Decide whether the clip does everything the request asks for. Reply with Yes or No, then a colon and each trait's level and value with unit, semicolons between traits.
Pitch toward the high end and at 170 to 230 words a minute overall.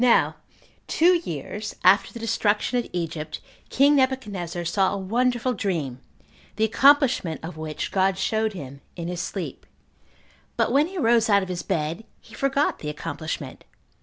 No: high, 200 Hz; average, 160 wpm